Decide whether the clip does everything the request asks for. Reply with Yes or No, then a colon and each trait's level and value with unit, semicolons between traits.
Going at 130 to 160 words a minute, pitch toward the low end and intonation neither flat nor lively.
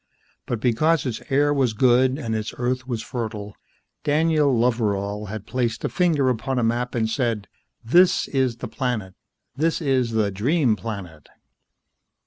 Yes: average, 150 wpm; low, 120 Hz; average, 3.4 semitones